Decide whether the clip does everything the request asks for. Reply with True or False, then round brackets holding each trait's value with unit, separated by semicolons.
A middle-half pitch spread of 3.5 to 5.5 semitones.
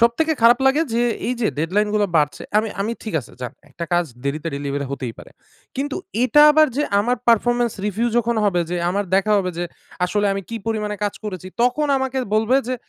True (5.0 semitones)